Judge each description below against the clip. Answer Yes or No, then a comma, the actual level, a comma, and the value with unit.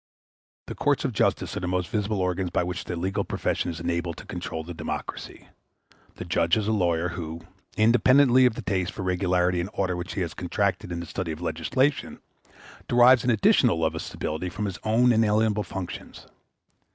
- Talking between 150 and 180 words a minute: No, average, 190 wpm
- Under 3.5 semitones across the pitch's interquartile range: No, average, 3.9 semitones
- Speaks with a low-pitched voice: Yes, very low, 90 Hz